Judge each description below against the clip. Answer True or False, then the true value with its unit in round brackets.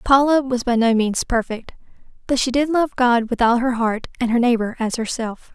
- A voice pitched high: True (245 Hz)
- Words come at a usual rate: False (215 wpm)